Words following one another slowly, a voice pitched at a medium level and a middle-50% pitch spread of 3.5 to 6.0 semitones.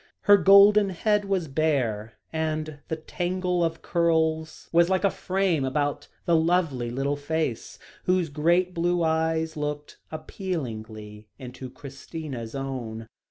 Yes: slow, 125 wpm; medium, 160 Hz; average, 4.4 semitones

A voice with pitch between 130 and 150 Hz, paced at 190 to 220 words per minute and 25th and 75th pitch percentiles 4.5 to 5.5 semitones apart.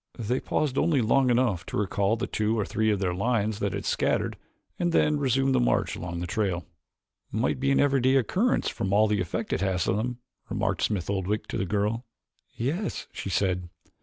No: low, 105 Hz; average, 200 wpm; average, 4.9 semitones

